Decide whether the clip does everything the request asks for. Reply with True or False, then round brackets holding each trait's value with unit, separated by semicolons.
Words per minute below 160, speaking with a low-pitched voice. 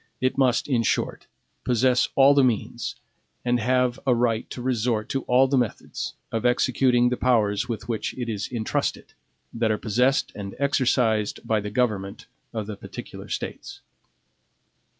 True (150 wpm; 120 Hz)